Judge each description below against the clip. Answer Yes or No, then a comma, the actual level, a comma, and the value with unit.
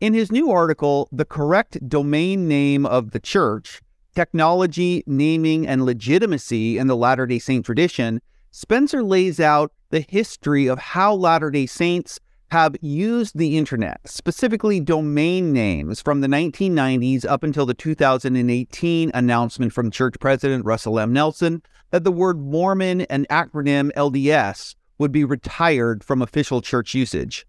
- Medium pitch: Yes, medium, 150 Hz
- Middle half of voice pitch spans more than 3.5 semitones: Yes, average, 4.7 semitones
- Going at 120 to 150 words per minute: Yes, average, 145 wpm